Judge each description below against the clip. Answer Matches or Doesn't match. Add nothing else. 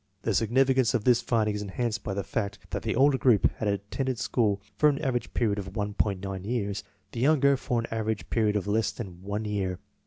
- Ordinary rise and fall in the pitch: Matches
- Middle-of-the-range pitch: Doesn't match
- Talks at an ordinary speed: Doesn't match